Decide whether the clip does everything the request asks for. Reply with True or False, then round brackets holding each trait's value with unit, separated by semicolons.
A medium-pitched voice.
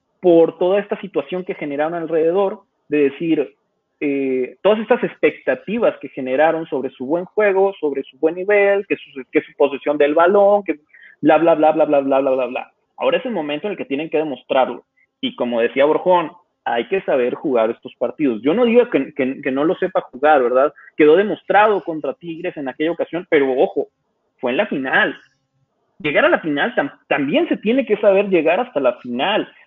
True (165 Hz)